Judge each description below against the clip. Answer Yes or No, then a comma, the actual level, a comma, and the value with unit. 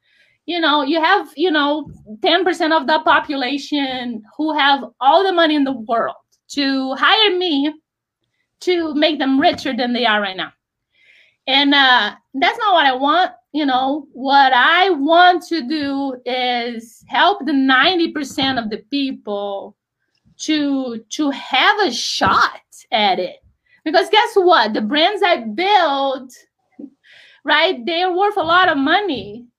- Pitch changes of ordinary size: Yes, average, 4.4 semitones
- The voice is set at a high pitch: Yes, very high, 290 Hz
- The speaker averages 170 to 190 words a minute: No, average, 145 wpm